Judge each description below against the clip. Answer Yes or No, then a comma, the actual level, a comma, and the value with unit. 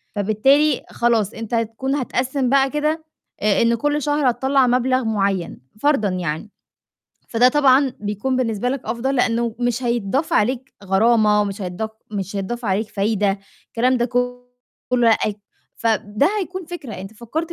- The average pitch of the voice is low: No, high, 235 Hz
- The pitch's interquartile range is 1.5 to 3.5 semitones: No, average, 4.0 semitones